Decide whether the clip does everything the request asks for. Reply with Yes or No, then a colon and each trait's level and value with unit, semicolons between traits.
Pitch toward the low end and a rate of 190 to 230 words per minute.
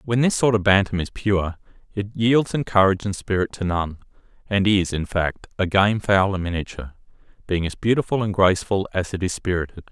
Yes: very low, 95 Hz; average, 200 wpm